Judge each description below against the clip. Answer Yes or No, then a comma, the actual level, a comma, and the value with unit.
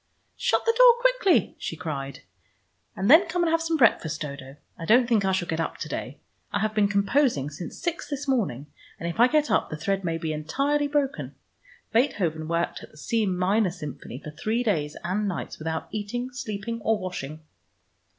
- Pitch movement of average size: No, wide, 8.1 semitones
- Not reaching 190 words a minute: No, average, 195 wpm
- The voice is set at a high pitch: Yes, high, 200 Hz